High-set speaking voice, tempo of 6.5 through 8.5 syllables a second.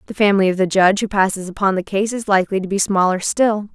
Yes: high, 195 Hz; 6.8 syllables/s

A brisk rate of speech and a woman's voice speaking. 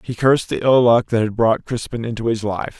No: fast, 255 wpm; male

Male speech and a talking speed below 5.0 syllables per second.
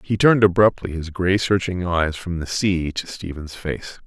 Yes: male; 4.6 syllables/s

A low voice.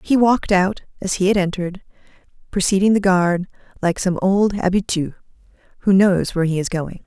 No: high, 190 Hz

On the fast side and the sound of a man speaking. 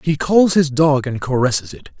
Yes: fast, 210 wpm; male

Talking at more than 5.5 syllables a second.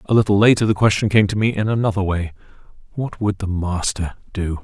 Yes: 6.0 syllables/s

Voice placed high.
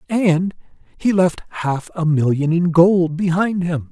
No: medium, 170 Hz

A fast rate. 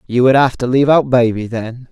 Yes: fast, 250 wpm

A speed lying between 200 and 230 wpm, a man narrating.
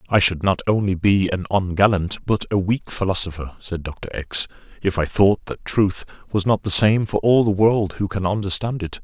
Yes: fast, 205 wpm; male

